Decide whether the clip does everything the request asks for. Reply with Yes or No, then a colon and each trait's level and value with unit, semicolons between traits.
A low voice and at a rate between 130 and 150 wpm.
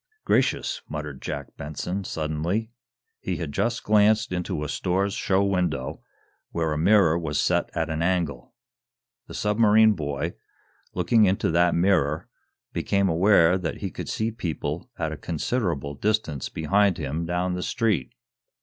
Yes: very low, 90 Hz; average, 145 wpm